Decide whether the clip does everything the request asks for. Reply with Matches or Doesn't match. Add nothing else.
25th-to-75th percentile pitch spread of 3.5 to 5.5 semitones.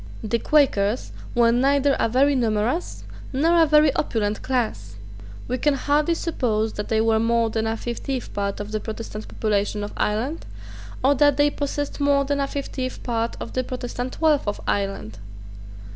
Matches